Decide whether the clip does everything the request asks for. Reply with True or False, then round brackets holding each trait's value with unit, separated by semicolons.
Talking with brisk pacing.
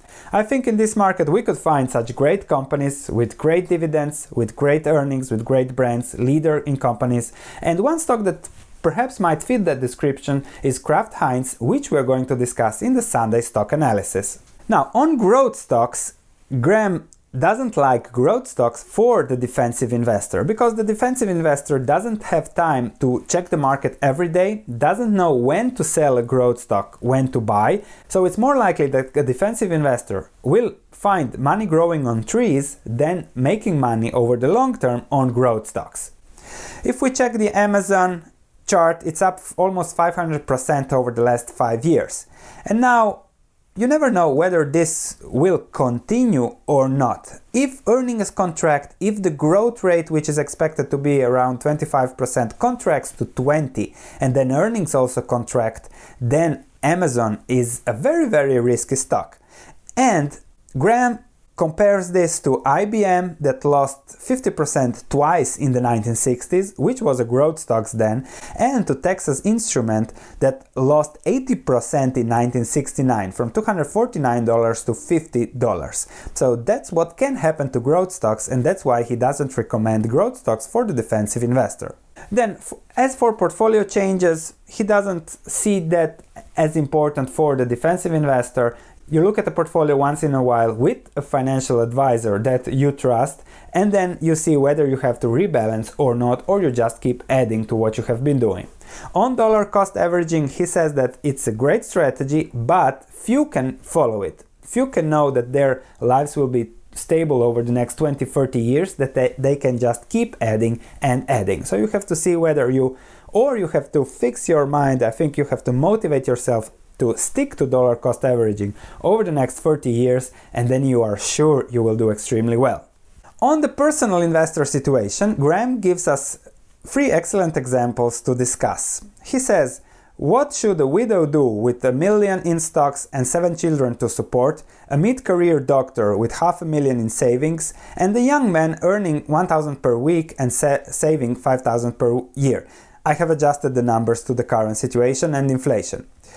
False (170 wpm)